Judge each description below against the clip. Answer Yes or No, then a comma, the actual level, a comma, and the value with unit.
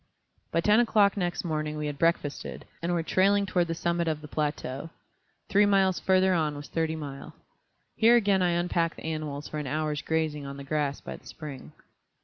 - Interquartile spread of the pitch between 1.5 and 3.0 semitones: No, average, 3.7 semitones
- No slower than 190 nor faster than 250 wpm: Yes, average, 195 wpm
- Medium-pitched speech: Yes, medium, 160 Hz